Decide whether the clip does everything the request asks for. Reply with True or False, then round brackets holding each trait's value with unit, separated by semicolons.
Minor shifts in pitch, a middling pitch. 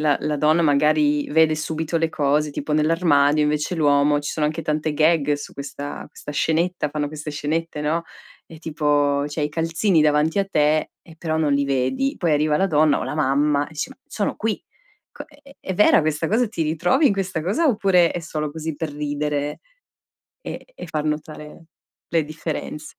True (1.9 semitones; 155 Hz)